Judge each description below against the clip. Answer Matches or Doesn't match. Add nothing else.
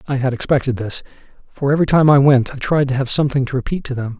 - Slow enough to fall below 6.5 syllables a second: Doesn't match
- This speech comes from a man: Matches